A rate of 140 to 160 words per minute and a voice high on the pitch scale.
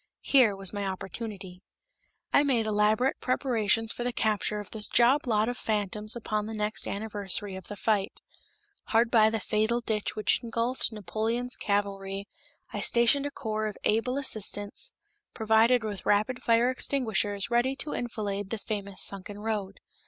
Yes: average, 155 wpm; high, 215 Hz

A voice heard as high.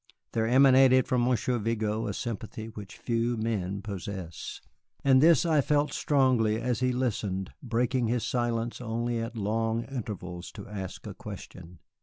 No: low, 115 Hz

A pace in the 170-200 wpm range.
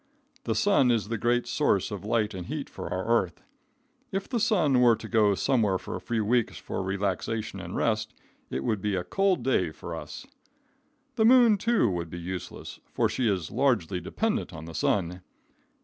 Yes: average, 190 wpm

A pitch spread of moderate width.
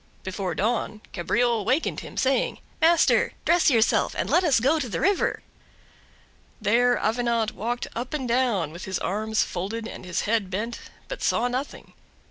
Yes: average, 3.5 semitones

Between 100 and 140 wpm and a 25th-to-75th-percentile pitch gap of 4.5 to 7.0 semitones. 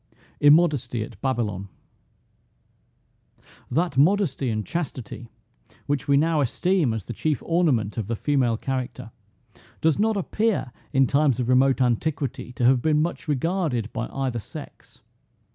Yes: slow, 135 wpm; average, 4.9 semitones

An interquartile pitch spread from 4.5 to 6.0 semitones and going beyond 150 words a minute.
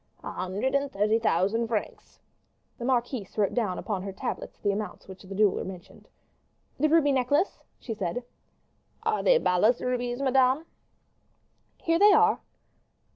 No: wide, 5.6 semitones; average, 145 wpm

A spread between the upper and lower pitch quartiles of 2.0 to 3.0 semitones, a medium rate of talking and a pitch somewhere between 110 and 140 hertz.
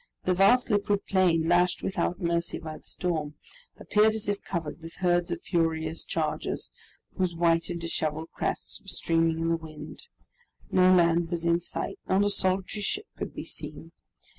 No: narrow, 2.4 semitones; average, 170 wpm; medium, 175 Hz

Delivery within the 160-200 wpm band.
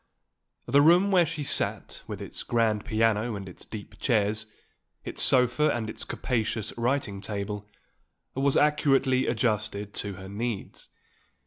No: slow, 135 wpm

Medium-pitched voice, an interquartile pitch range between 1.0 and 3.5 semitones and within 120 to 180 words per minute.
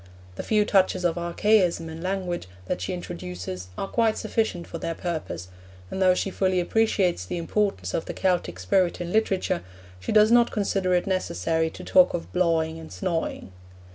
Yes: medium, 175 Hz; average, 3.2 semitones; average, 175 wpm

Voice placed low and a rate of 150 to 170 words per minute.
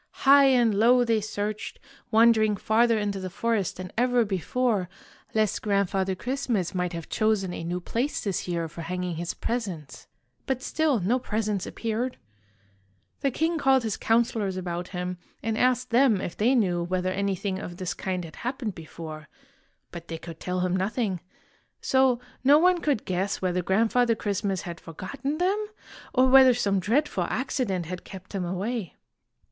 No: high, 205 Hz; average, 165 wpm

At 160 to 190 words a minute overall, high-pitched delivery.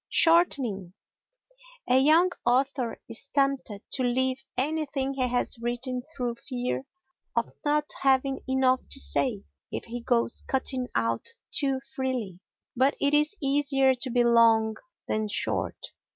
No: slow, 135 wpm; very high, 260 Hz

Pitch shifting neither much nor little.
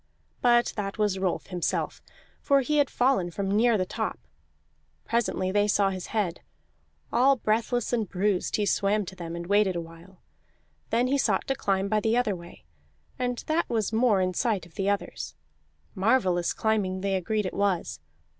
Yes: average, 3.8 semitones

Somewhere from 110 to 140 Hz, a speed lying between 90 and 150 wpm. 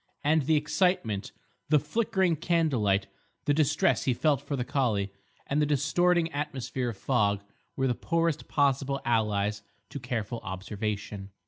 Yes: low, 135 Hz; average, 140 wpm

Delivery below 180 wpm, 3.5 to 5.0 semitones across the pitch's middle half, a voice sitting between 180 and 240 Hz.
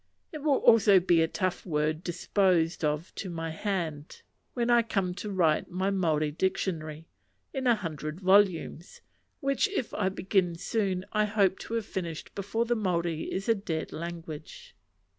Yes: average, 160 wpm; average, 4.2 semitones; medium, 185 Hz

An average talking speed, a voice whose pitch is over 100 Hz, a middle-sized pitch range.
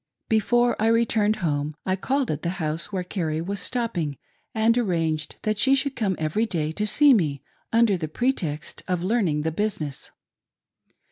No: average, 160 wpm; high, 190 Hz; wide, 6.3 semitones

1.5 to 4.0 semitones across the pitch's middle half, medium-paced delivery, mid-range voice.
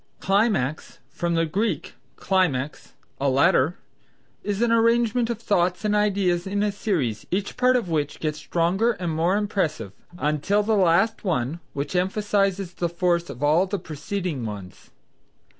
No: average, 4.7 semitones; average, 150 wpm; medium, 180 Hz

